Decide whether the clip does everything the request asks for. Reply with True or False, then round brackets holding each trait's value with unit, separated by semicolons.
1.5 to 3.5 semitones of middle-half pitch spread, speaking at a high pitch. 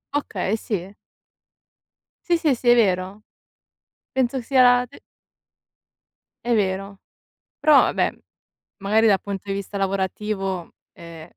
False (4.1 semitones; 205 Hz)